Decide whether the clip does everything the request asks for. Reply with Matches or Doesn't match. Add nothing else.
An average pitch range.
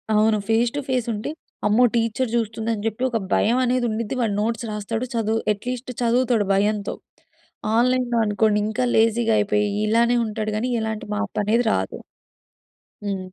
Doesn't match